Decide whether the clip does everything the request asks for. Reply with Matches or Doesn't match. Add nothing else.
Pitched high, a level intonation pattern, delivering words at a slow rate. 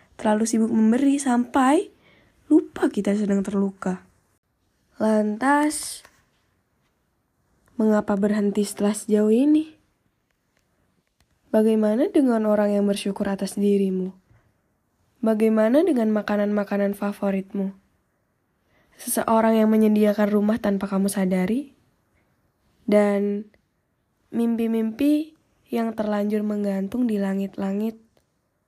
Matches